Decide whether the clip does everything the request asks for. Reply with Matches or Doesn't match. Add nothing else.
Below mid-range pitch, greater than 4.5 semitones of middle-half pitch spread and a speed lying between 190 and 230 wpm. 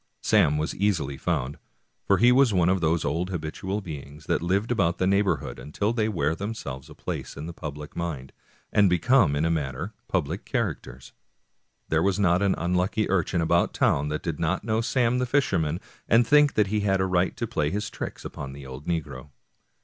Matches